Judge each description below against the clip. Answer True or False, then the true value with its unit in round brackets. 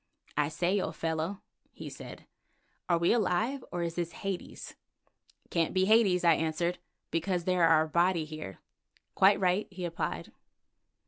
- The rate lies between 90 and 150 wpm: True (145 wpm)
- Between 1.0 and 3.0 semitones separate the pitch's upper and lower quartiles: True (2.5 semitones)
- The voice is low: False (175 Hz)